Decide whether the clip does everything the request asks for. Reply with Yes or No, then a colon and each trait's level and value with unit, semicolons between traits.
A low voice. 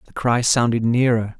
Yes: low, 120 Hz